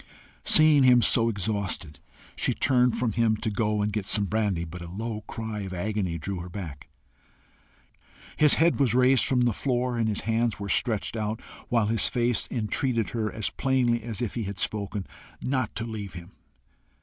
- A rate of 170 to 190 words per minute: Yes, average, 185 wpm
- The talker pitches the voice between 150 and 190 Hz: No, low, 110 Hz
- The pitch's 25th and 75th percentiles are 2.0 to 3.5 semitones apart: Yes, average, 3.2 semitones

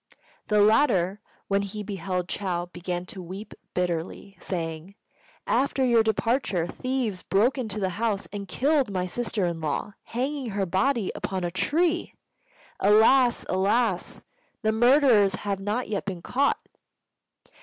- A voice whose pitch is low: No, high, 205 Hz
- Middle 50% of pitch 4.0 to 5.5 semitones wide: Yes, average, 4.5 semitones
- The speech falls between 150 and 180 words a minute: No, slow, 135 wpm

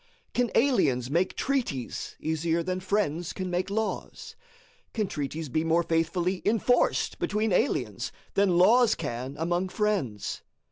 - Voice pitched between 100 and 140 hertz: No, medium, 180 Hz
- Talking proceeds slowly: Yes, slow, 130 wpm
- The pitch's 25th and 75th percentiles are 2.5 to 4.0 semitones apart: No, average, 4.7 semitones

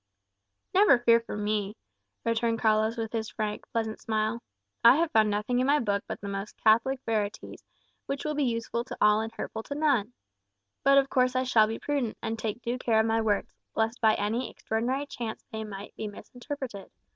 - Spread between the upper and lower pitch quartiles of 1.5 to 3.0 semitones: Yes, average, 2.7 semitones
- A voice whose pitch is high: Yes, high, 225 Hz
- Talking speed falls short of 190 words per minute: No, average, 195 wpm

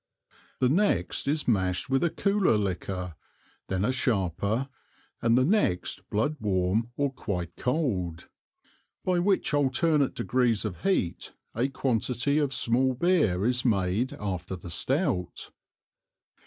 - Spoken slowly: Yes, slow, 130 wpm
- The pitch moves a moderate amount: No, wide, 7.1 semitones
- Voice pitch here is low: Yes, low, 120 Hz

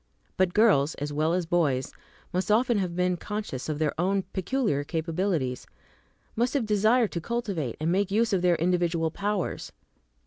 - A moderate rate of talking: Yes, average, 165 wpm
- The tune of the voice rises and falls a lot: No, average, 4.5 semitones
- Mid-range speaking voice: Yes, medium, 180 Hz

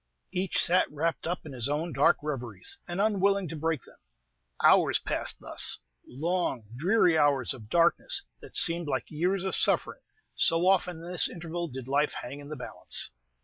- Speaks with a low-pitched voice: No, medium, 165 Hz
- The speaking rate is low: No, average, 175 wpm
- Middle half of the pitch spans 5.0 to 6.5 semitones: No, average, 3.9 semitones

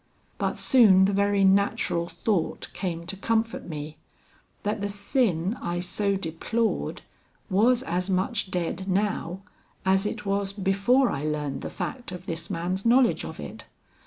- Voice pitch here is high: Yes, high, 195 Hz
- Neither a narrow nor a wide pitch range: Yes, average, 3.0 semitones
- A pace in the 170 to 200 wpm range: No, average, 150 wpm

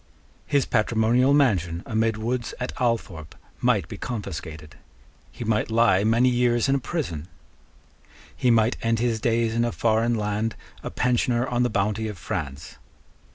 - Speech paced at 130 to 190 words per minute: Yes, average, 155 wpm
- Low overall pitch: Yes, low, 115 Hz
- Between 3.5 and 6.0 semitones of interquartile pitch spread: No, narrow, 2.6 semitones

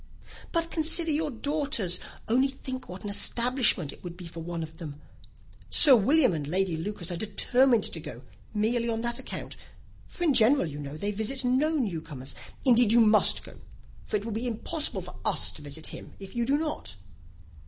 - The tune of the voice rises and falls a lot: Yes, wide, 7.3 semitones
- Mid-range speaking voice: No, high, 220 Hz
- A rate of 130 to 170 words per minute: No, average, 195 wpm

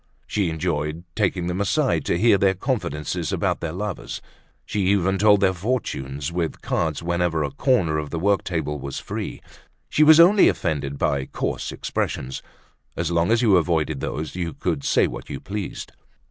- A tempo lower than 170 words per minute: No, average, 175 wpm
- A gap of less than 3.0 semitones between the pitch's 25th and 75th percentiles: No, average, 4.6 semitones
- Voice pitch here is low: Yes, very low, 85 Hz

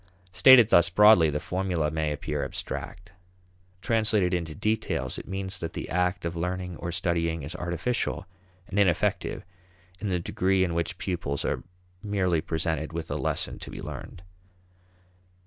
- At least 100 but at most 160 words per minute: Yes, average, 150 wpm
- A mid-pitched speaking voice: No, very low, 90 Hz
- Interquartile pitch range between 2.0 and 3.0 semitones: Yes, narrow, 2.6 semitones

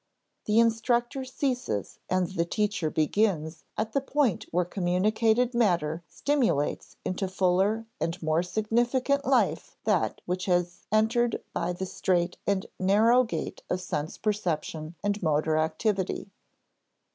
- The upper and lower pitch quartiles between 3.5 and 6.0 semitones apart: Yes, average, 4.7 semitones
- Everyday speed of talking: No, slow, 125 wpm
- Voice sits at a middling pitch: No, high, 195 Hz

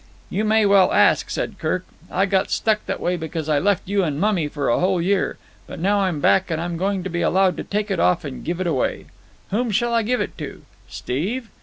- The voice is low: No, high, 190 Hz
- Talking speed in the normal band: No, fast, 230 wpm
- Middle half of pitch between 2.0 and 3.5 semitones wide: Yes, average, 3.2 semitones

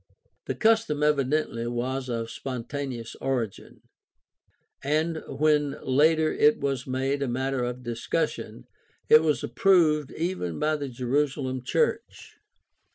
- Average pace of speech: No, slow, 115 wpm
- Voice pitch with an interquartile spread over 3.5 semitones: No, average, 3.2 semitones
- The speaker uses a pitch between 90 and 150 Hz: Yes, medium, 140 Hz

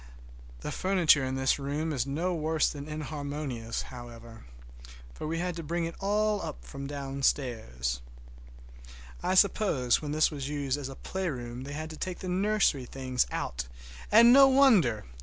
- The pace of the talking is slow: No, average, 160 wpm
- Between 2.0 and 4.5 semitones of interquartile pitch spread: No, average, 5.2 semitones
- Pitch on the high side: No, medium, 145 Hz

